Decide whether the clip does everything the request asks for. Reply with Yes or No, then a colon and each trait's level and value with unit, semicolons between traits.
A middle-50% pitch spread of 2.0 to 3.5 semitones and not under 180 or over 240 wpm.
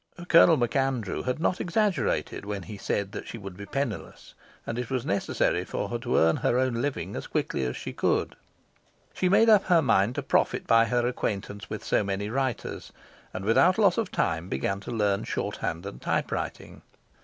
No: wide, 5.6 semitones; average, 185 wpm